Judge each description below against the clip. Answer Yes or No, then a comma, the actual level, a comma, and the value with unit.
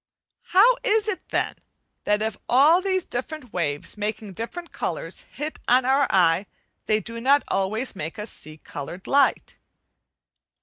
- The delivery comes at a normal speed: Yes, average, 145 wpm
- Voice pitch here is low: No, high, 230 Hz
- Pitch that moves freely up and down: Yes, wide, 7.5 semitones